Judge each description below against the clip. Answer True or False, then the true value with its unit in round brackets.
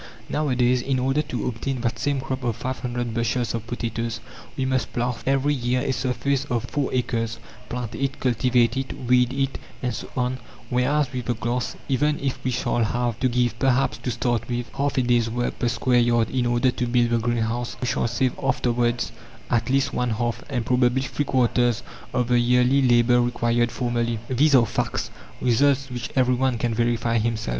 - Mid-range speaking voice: False (125 Hz)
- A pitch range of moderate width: False (1.6 semitones)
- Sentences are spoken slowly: False (190 wpm)